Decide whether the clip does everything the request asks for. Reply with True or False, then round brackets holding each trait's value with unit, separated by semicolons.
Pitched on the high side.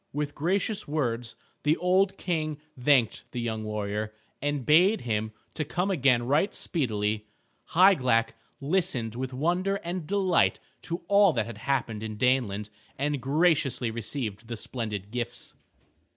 False (135 Hz)